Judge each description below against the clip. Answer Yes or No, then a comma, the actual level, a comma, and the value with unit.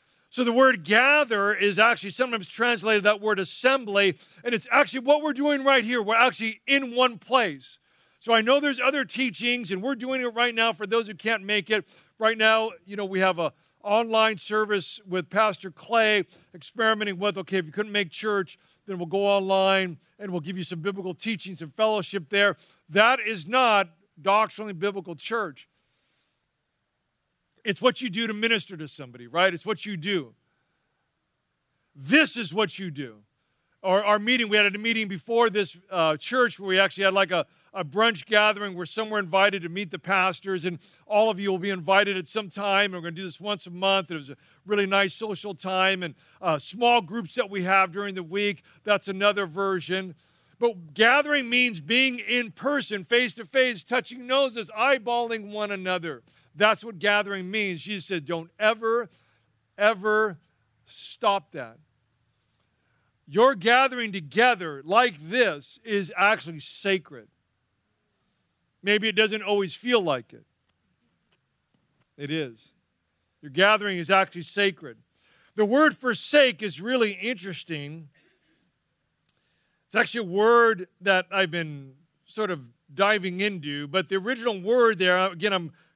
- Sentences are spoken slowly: No, average, 165 wpm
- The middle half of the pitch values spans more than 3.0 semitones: Yes, average, 4.1 semitones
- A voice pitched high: Yes, high, 200 Hz